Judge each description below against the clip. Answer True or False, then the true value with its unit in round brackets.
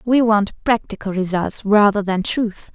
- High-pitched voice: True (210 Hz)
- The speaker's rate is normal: True (155 wpm)